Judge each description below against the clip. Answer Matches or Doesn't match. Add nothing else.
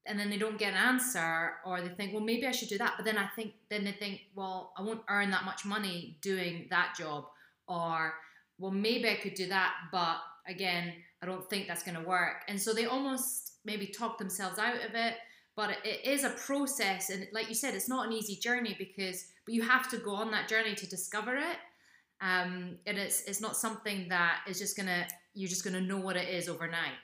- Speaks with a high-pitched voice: Matches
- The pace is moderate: Doesn't match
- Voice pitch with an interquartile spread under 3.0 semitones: Doesn't match